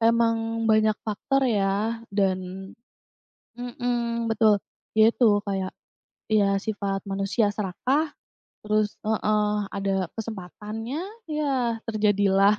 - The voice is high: Yes, high, 215 Hz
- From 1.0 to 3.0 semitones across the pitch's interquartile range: Yes, narrow, 2.6 semitones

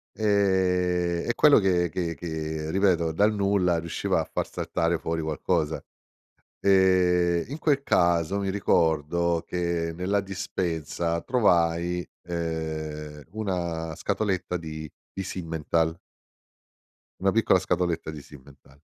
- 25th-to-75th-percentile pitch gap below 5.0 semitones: Yes, average, 2.7 semitones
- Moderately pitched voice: No, very low, 85 Hz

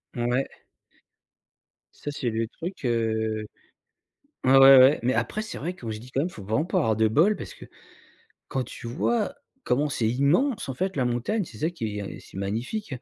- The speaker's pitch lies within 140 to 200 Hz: No, low, 130 Hz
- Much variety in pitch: Yes, wide, 5.9 semitones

